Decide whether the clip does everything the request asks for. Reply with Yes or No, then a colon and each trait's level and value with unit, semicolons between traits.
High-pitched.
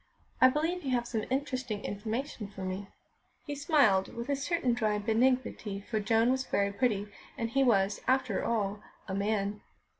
Yes: high, 230 Hz